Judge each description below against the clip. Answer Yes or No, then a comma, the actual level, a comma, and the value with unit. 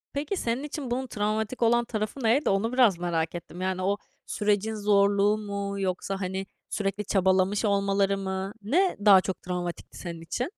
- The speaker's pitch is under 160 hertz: No, high, 200 Hz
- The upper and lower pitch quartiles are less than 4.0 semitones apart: Yes, average, 2.9 semitones